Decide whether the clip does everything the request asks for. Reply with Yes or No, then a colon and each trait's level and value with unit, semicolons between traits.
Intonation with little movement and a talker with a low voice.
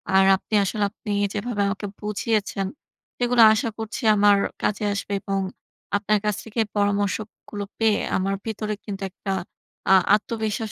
No: narrow, 1.6 semitones; high, 210 Hz